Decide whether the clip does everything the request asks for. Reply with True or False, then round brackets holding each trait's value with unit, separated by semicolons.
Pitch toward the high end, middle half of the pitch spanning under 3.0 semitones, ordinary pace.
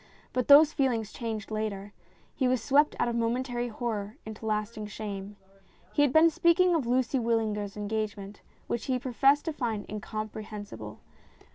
False (230 Hz; 3.5 semitones; 155 wpm)